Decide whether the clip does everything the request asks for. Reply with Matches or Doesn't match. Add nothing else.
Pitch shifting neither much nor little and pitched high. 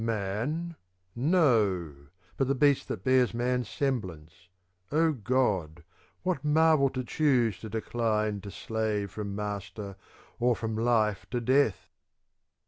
Doesn't match